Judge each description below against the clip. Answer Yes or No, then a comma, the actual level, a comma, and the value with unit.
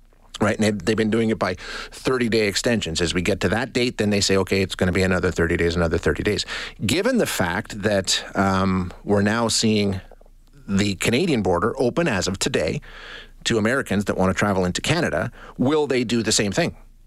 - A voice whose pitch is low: Yes, low, 100 Hz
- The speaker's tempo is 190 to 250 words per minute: Yes, fast, 205 wpm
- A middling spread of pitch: Yes, average, 3.0 semitones